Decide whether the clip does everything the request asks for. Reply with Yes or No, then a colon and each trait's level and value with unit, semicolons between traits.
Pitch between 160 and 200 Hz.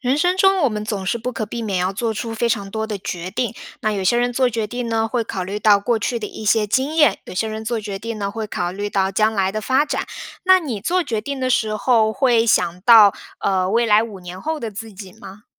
No: high, 220 Hz